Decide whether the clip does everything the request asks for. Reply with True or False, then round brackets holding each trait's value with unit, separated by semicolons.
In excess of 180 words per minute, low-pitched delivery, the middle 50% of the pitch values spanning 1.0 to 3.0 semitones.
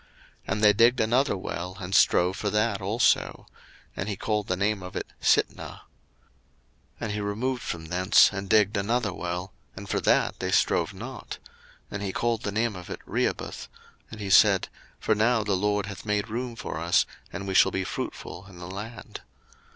True (190 wpm; 100 Hz; 2.5 semitones)